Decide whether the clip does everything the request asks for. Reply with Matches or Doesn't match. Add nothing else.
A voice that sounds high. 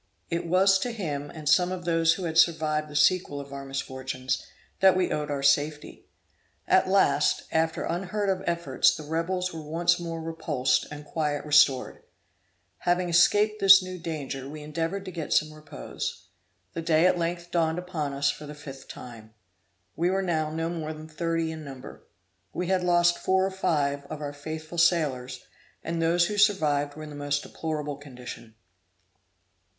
Doesn't match